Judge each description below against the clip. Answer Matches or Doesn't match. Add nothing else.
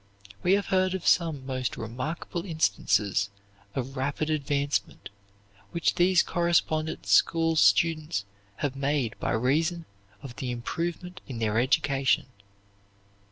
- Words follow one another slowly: Matches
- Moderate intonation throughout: Matches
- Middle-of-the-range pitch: Matches